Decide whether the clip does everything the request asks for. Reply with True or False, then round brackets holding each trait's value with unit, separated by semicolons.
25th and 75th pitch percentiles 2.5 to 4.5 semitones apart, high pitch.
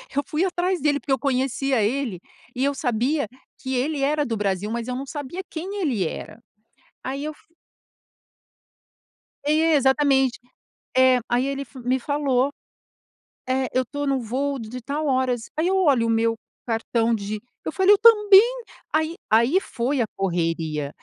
True (3.9 semitones; 265 Hz)